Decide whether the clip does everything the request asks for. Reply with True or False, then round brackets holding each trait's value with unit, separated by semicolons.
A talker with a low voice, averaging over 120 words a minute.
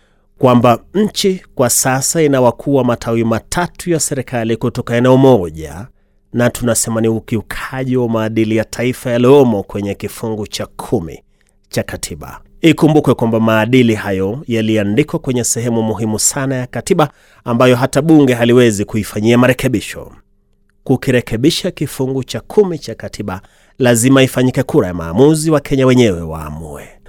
True (120 Hz; 130 wpm)